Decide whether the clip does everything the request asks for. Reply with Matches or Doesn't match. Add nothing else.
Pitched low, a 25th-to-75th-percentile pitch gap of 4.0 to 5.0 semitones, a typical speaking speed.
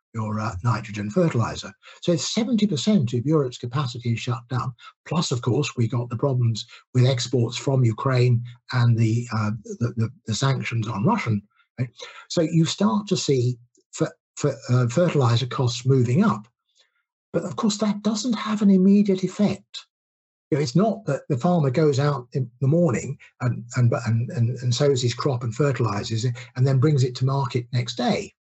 Matches